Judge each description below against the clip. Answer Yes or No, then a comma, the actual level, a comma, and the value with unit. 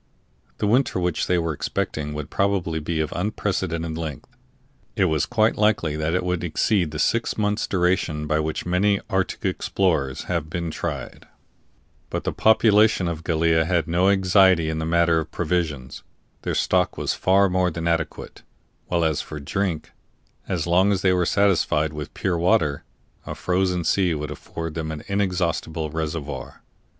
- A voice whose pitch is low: Yes, very low, 85 Hz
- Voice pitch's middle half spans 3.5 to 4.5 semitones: No, average, 3.1 semitones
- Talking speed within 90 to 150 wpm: No, average, 165 wpm